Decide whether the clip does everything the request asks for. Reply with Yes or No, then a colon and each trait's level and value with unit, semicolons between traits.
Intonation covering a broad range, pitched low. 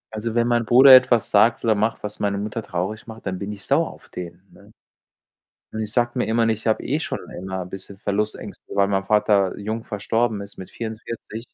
No: narrow, 2.5 semitones; low, 110 Hz